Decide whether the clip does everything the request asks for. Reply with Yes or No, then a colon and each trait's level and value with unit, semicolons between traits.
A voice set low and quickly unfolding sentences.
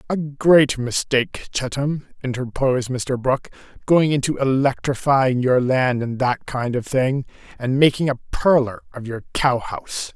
No: low, 130 Hz; average, 150 wpm